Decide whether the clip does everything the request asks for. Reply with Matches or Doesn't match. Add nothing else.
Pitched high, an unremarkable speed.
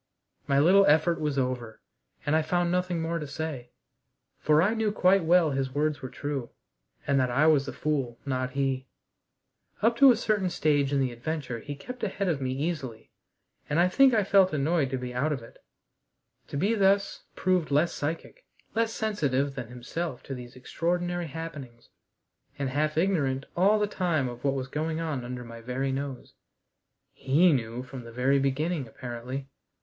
Doesn't match